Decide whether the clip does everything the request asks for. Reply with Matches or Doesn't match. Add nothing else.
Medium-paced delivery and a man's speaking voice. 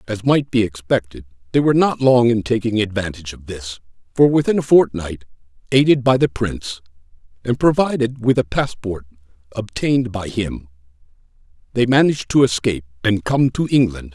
Matches